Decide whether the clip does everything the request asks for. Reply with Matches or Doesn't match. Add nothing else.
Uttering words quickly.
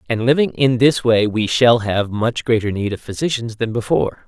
Matches